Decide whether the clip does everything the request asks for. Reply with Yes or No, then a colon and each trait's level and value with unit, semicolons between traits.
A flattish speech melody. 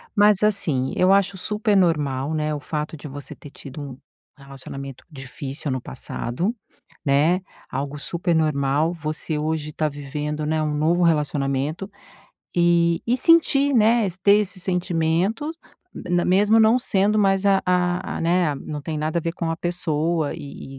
No: average, 4.4 semitones